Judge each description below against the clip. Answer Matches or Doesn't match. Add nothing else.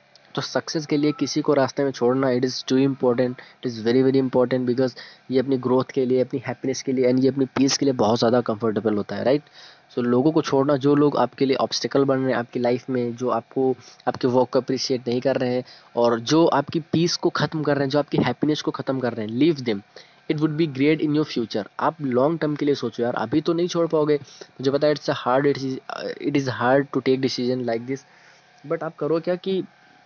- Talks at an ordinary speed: Doesn't match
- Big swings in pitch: Doesn't match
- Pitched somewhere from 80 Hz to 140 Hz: Matches